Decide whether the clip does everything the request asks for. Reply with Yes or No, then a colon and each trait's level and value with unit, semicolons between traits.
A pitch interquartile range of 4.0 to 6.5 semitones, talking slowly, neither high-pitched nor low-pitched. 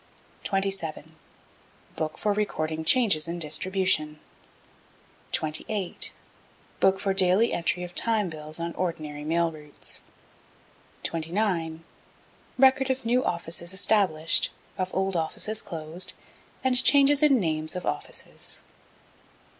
Yes: average, 4.5 semitones; slow, 105 wpm; medium, 180 Hz